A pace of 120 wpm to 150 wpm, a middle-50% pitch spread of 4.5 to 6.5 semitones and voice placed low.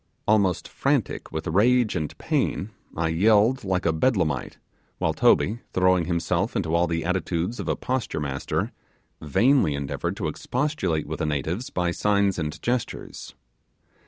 Yes: average, 145 wpm; average, 5.1 semitones; very low, 90 Hz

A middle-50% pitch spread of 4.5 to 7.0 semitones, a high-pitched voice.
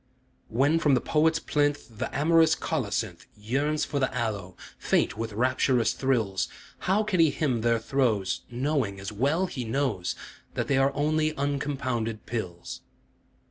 No: average, 5.0 semitones; low, 130 Hz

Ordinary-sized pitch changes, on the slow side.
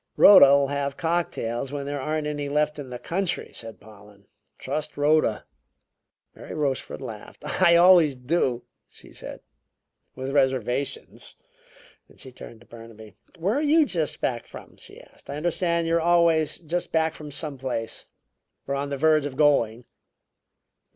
No: average, 4.2 semitones; average, 155 wpm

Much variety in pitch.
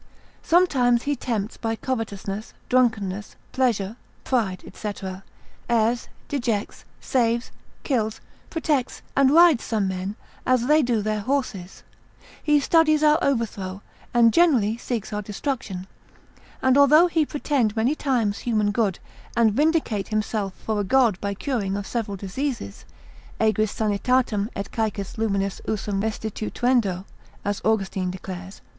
No: average, 4.4 semitones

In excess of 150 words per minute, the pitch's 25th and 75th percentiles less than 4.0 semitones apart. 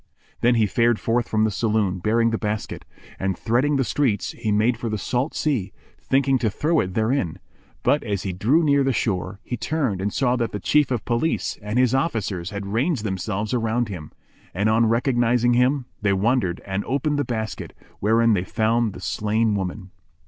Yes: average, 190 wpm; average, 3.4 semitones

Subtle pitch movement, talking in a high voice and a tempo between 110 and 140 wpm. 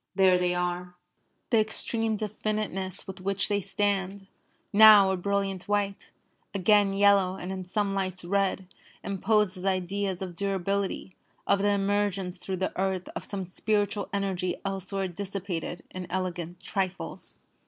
Yes: narrow, 1.6 semitones; high, 195 Hz; slow, 135 wpm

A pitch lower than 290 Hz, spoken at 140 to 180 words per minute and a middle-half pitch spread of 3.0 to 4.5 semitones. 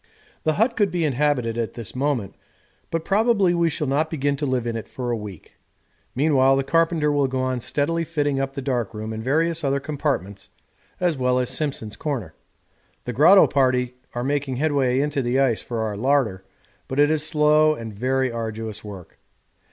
No: low, 135 Hz; average, 190 wpm; average, 4.0 semitones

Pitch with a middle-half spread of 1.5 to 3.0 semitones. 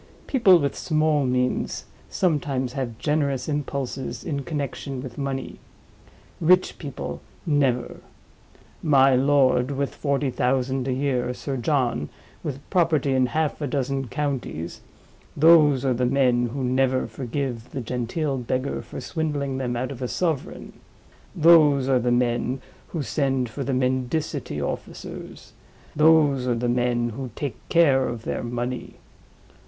Yes: narrow, 2.6 semitones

